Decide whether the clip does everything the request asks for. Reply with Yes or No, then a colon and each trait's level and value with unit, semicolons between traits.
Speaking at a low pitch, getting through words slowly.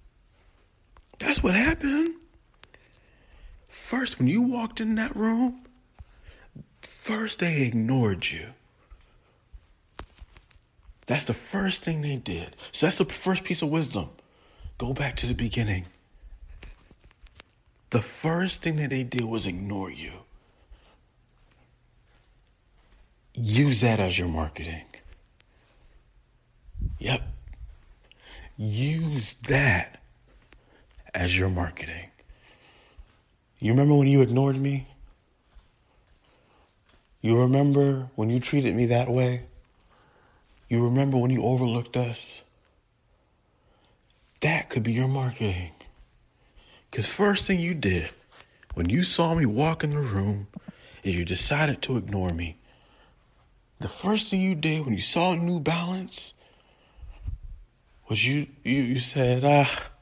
Yes: low, 125 Hz; slow, 110 wpm